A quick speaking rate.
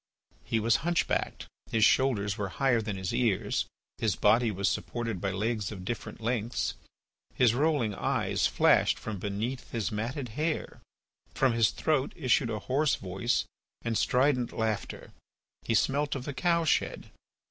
No: average, 155 wpm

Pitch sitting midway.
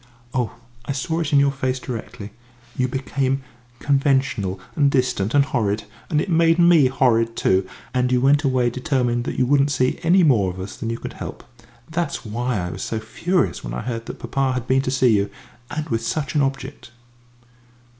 No: low, 130 Hz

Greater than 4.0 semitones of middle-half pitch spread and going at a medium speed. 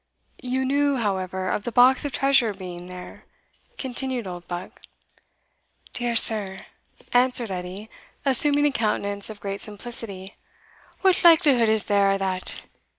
No: average, 5.1 semitones; slow, 125 wpm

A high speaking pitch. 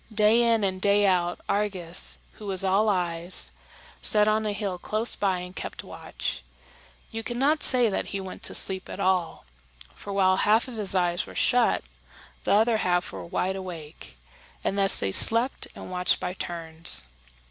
Yes: high, 195 Hz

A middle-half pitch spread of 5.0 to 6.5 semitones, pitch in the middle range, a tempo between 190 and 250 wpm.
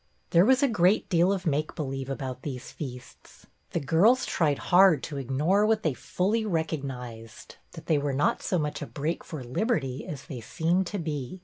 Yes: wide, 5.5 semitones; medium, 155 Hz; average, 195 wpm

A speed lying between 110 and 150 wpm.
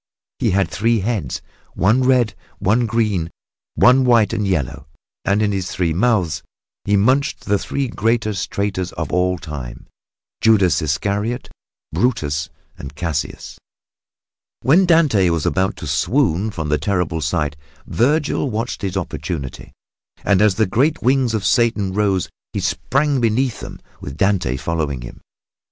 Yes: average, 145 wpm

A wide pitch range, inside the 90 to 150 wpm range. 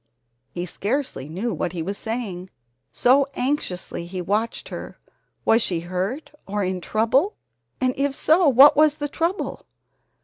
Yes: wide, 7.4 semitones; average, 145 wpm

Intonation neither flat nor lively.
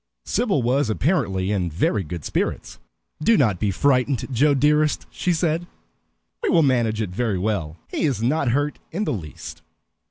No: wide, 6.8 semitones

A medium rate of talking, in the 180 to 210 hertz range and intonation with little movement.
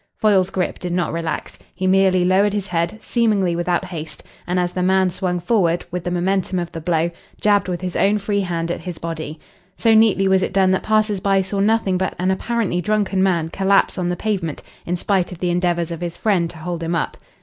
No: fast, 225 wpm; medium, 185 Hz; narrow, 2.2 semitones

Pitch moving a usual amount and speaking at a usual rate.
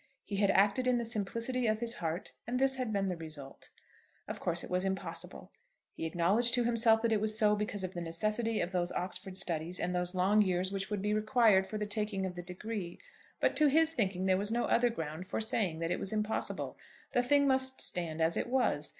No: average, 4.3 semitones; fast, 225 wpm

